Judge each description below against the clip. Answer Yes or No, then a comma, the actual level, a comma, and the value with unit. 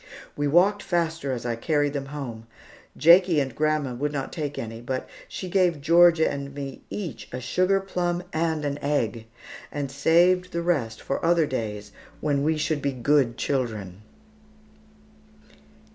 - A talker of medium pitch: Yes, medium, 145 Hz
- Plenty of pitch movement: No, average, 4.5 semitones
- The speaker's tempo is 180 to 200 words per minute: No, average, 155 wpm